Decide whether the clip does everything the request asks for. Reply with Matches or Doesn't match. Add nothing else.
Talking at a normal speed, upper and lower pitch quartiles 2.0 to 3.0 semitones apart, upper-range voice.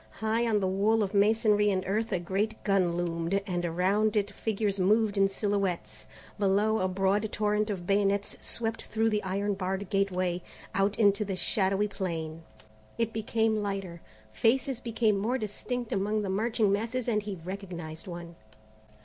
Matches